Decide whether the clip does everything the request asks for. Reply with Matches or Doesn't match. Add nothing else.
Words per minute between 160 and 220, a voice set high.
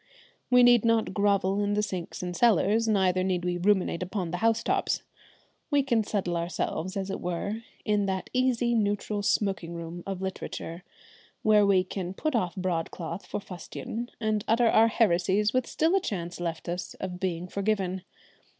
Matches